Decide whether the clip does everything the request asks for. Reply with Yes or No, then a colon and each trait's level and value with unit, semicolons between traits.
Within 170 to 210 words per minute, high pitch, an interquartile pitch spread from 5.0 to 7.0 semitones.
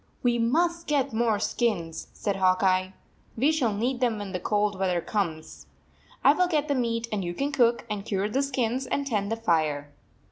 Yes: average, 190 wpm; high, 225 Hz; average, 5.3 semitones